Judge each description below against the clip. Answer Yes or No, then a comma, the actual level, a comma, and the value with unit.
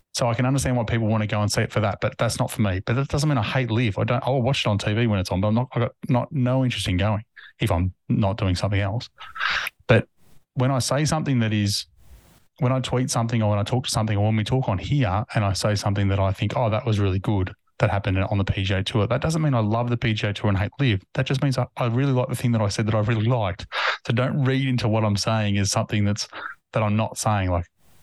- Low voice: Yes, low, 110 Hz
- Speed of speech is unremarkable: No, fast, 290 wpm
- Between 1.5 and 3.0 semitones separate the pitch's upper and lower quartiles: No, average, 3.4 semitones